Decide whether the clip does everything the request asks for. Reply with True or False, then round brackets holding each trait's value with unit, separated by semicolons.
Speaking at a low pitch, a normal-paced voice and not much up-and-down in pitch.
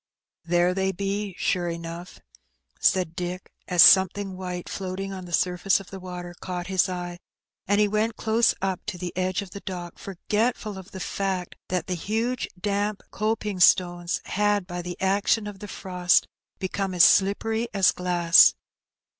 False (190 Hz; 170 wpm; 2.2 semitones)